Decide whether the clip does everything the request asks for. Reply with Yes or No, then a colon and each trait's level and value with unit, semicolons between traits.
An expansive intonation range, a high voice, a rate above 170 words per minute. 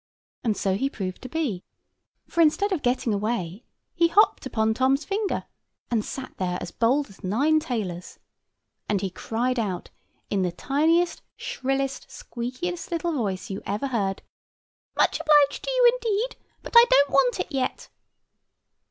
No: wide, 7.2 semitones; very high, 255 Hz; average, 155 wpm